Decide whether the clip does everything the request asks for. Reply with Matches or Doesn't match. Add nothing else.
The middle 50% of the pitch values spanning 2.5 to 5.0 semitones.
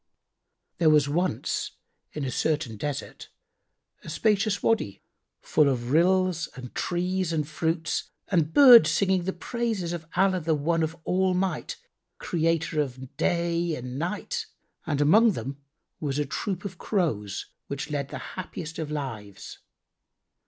Matches